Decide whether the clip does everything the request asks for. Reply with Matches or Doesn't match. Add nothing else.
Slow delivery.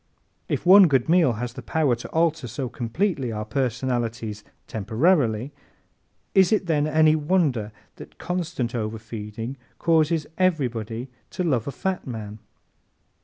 Matches